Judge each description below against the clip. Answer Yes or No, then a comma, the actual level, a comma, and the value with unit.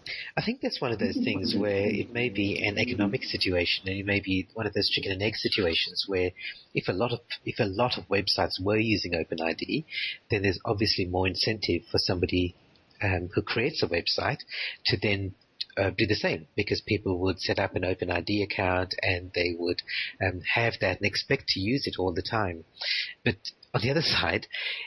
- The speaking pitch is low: Yes, low, 100 Hz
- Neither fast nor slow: No, fast, 210 wpm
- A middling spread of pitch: Yes, average, 3.1 semitones